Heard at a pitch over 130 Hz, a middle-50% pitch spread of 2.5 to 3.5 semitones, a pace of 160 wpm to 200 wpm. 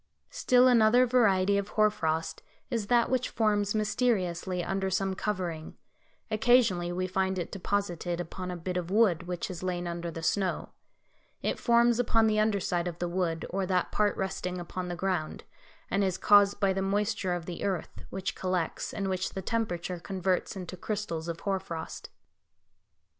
Yes: high, 190 Hz; average, 3.0 semitones; average, 170 wpm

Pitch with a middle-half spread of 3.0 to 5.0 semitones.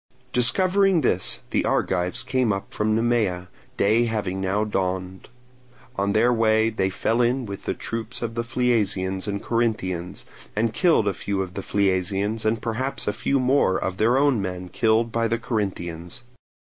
Yes: average, 3.7 semitones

